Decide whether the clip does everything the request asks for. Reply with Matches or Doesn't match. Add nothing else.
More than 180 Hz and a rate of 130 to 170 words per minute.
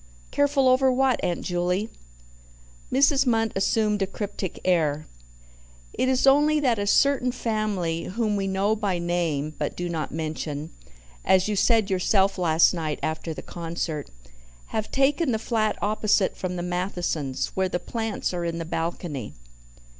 Matches